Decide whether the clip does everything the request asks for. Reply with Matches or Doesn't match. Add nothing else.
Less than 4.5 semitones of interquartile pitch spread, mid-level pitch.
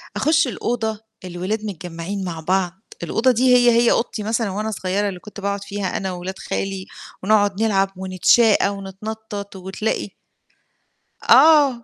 Doesn't match